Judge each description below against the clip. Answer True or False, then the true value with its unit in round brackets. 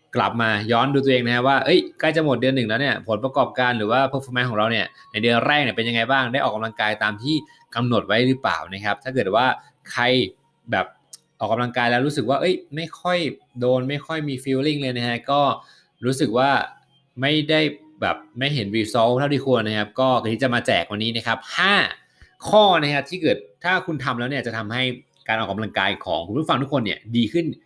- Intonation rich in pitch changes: False (3.7 semitones)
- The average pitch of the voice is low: True (130 Hz)